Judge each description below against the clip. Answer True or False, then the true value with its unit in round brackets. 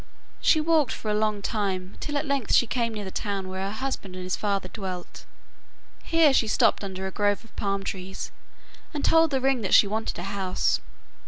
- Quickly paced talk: True (210 wpm)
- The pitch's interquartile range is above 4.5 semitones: True (5.2 semitones)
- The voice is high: True (205 Hz)